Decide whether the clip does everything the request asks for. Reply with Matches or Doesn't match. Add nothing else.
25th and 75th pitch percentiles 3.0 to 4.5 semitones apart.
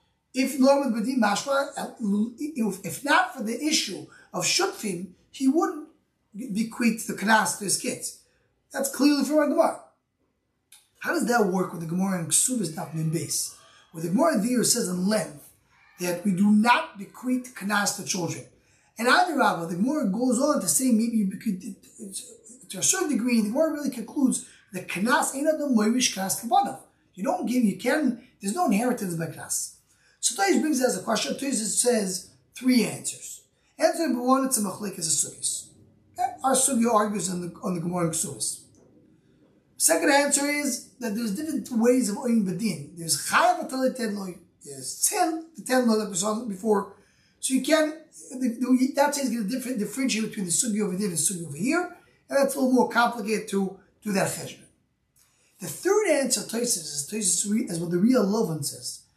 Doesn't match